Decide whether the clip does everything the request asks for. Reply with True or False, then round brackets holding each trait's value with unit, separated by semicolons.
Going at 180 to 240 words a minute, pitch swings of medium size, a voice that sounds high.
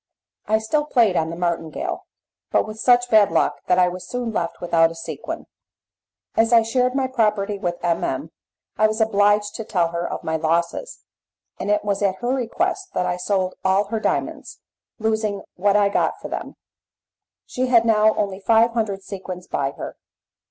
True (185 wpm; 4.0 semitones; 205 Hz)